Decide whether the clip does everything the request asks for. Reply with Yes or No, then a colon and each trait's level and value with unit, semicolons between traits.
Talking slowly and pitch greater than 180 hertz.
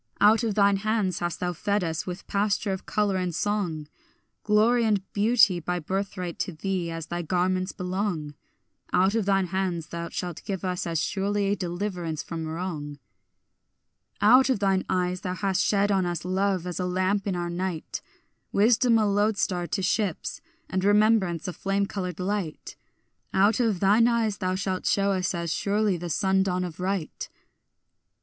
No: average, 170 wpm; high, 190 Hz